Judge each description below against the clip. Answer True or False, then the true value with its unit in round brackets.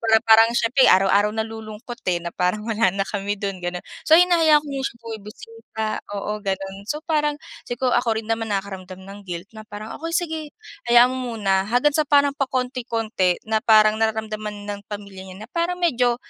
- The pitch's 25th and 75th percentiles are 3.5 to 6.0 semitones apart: True (3.9 semitones)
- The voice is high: True (220 Hz)